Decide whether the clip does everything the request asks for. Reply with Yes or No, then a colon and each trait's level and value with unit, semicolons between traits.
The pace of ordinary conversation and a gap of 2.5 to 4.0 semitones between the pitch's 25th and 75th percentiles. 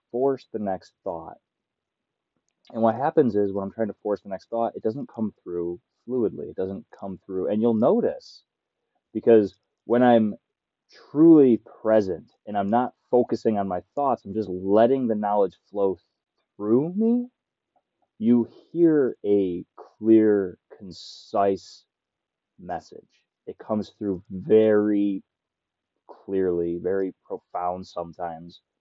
No: slow, 130 wpm; average, 3.4 semitones